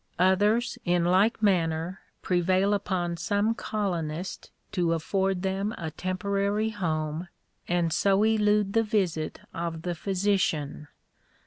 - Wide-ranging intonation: No, average, 3.2 semitones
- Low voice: No, medium, 185 Hz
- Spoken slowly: Yes, slow, 115 wpm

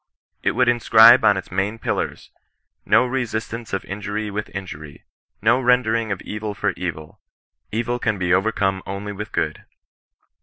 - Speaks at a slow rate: No, average, 165 wpm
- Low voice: Yes, low, 105 Hz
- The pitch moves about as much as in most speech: Yes, average, 3.1 semitones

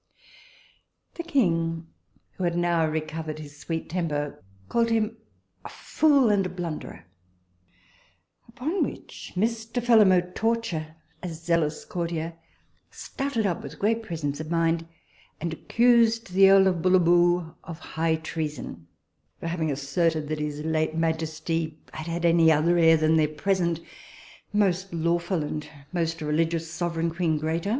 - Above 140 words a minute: No, slow, 135 wpm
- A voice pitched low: No, medium, 165 Hz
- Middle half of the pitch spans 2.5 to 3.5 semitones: Yes, average, 2.9 semitones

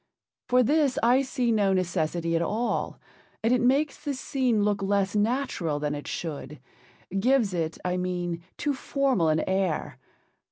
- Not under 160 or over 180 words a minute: No, average, 150 wpm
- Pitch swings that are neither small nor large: No, wide, 6.8 semitones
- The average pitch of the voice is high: Yes, high, 200 Hz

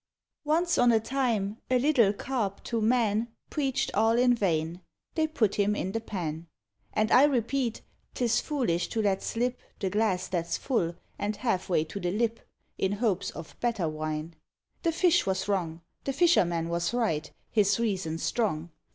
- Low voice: No, high, 210 Hz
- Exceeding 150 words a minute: Yes, average, 170 wpm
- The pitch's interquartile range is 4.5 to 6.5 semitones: Yes, wide, 5.5 semitones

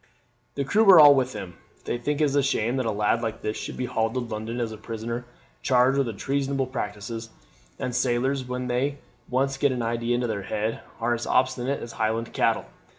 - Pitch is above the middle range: No, low, 120 Hz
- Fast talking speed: Yes, fast, 210 wpm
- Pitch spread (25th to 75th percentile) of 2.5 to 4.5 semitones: Yes, average, 3.0 semitones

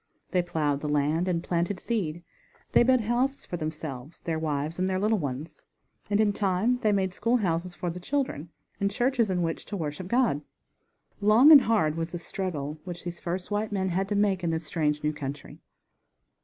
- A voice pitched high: No, medium, 180 Hz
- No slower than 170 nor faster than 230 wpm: Yes, average, 195 wpm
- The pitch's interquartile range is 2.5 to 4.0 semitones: No, average, 4.7 semitones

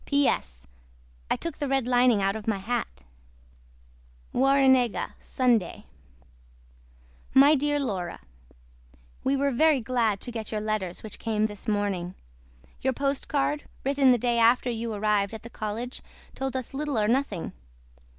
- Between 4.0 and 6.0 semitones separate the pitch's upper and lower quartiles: Yes, average, 4.3 semitones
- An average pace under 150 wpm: Yes, average, 140 wpm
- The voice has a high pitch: Yes, high, 240 Hz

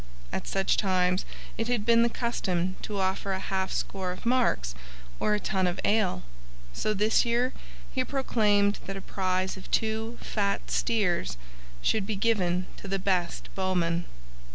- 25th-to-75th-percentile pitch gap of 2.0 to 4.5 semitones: Yes, average, 3.1 semitones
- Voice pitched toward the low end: No, high, 195 Hz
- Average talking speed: Yes, average, 160 wpm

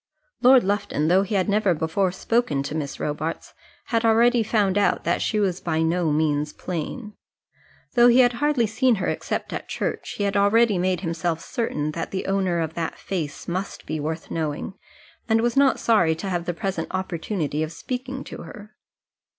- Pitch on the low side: No, high, 190 Hz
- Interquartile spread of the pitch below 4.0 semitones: No, wide, 5.5 semitones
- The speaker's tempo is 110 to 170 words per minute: No, average, 185 wpm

